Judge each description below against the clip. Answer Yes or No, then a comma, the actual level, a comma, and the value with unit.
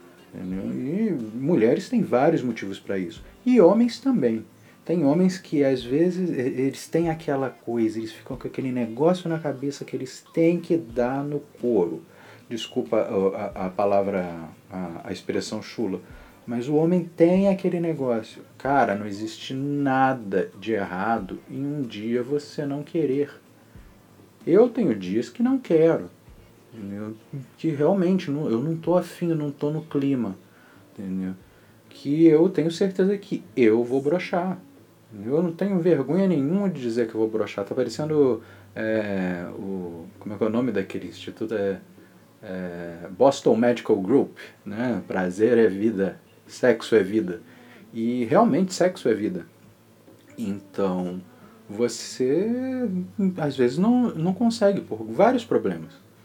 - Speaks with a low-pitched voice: Yes, low, 130 Hz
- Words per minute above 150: No, average, 145 wpm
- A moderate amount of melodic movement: No, wide, 7.2 semitones